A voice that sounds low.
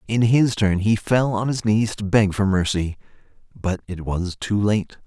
Yes: low, 105 Hz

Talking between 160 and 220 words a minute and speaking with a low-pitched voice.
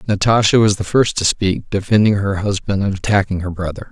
Yes: average, 200 wpm; low, 100 Hz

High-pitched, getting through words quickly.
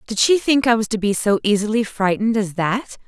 Yes: high, 220 Hz; fast, 235 wpm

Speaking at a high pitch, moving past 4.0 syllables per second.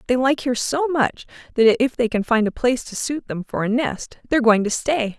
Yes: high, 245 Hz; 5.4 syllables/s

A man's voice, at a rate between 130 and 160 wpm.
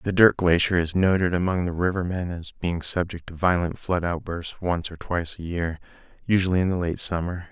No: male; fast, 205 wpm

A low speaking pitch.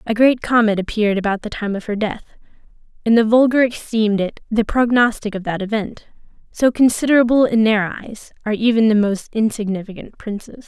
No: high, 220 Hz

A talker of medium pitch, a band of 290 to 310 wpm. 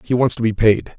No: low, 115 Hz; fast, 305 wpm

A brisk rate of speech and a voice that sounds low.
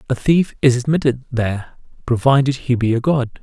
No: average, 175 wpm; low, 130 Hz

